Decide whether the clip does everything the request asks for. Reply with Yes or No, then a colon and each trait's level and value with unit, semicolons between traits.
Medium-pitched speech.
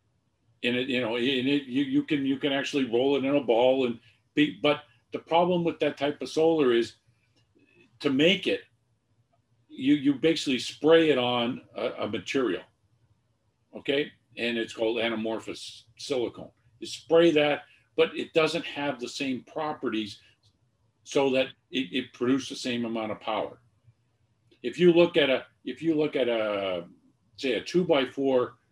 No: low, 125 Hz